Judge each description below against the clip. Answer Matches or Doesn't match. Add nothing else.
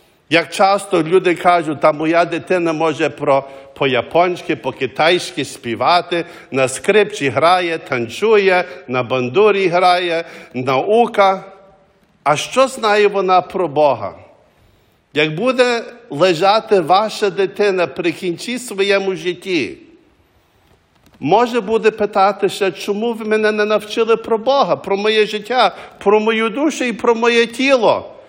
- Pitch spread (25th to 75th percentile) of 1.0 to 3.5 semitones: Doesn't match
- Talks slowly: Matches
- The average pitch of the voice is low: Doesn't match